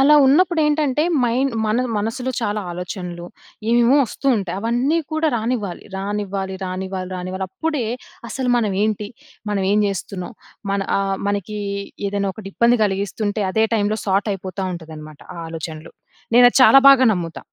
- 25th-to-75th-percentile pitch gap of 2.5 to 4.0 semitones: No, average, 4.4 semitones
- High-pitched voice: Yes, high, 205 Hz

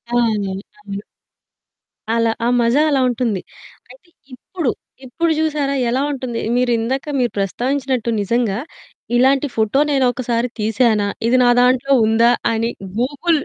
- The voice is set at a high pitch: Yes, high, 245 Hz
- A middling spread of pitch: Yes, average, 3.0 semitones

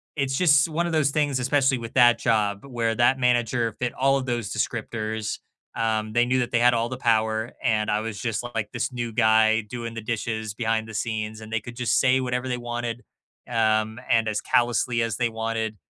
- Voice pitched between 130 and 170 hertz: No, low, 115 Hz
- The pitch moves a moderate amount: No, narrow, 2.1 semitones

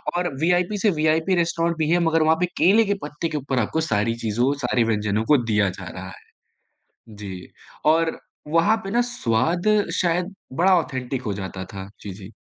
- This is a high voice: No, medium, 155 Hz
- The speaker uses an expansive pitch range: Yes, wide, 7.6 semitones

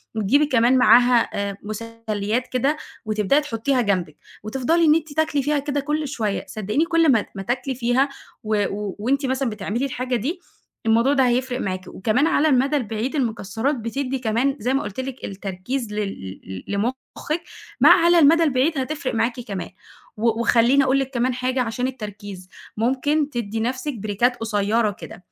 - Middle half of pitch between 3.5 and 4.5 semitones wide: Yes, average, 4.2 semitones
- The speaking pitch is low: No, high, 245 Hz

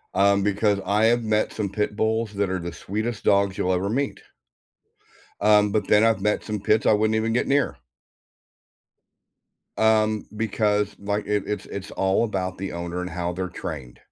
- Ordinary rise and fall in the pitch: No, narrow, 2.1 semitones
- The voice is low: Yes, low, 105 Hz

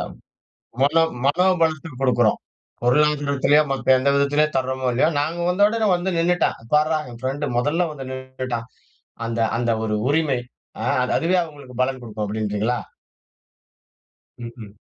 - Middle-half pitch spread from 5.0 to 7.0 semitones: No, average, 4.1 semitones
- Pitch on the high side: No, low, 135 Hz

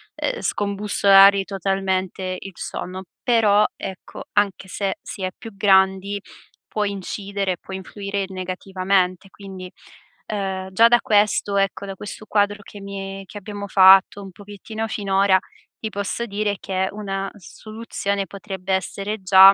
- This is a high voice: Yes, high, 195 Hz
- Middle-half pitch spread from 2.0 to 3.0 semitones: No, narrow, 1.2 semitones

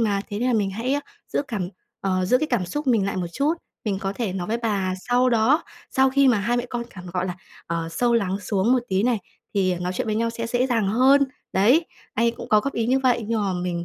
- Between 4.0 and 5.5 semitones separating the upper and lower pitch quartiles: Yes, average, 4.4 semitones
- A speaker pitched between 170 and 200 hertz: No, high, 220 Hz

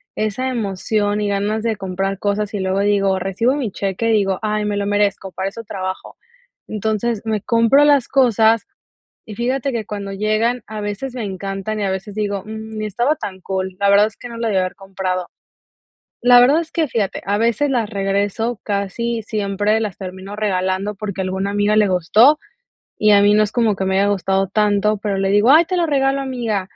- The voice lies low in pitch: No, high, 210 Hz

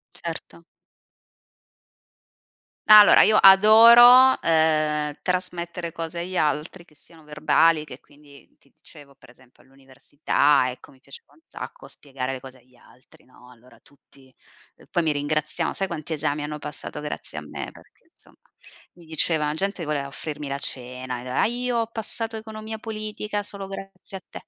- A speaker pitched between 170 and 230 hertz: No, medium, 155 Hz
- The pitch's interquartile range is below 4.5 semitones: No, wide, 5.6 semitones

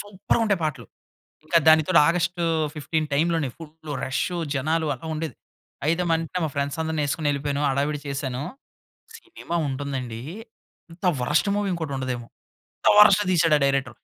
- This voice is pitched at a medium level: Yes, medium, 155 Hz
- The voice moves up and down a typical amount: Yes, average, 3.2 semitones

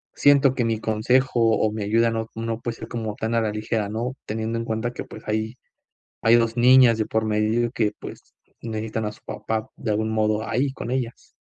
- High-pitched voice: No, low, 115 Hz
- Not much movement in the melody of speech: Yes, narrow, 1.4 semitones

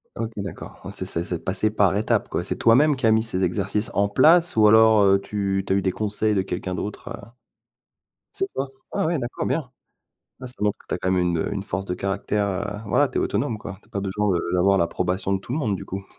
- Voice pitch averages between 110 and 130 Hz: No, low, 100 Hz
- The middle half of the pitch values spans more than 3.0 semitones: No, narrow, 2.6 semitones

